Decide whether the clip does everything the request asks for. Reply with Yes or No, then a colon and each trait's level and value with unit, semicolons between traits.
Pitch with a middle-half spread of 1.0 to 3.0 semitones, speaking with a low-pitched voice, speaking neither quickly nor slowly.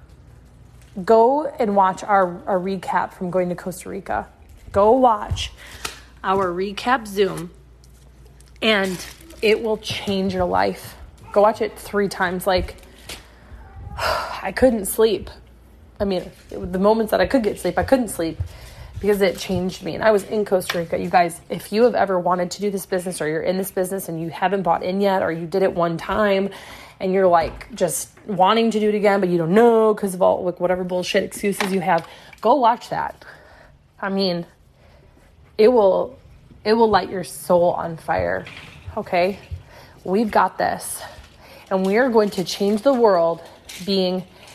No: average, 2.7 semitones; high, 190 Hz; average, 180 wpm